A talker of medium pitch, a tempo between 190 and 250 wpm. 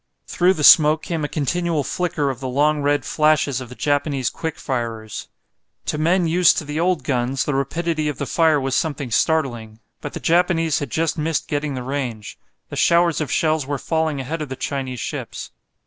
Yes: medium, 150 Hz; average, 195 wpm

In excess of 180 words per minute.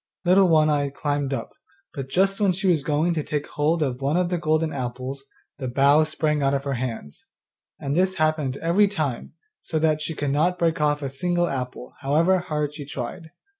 Yes: fast, 205 wpm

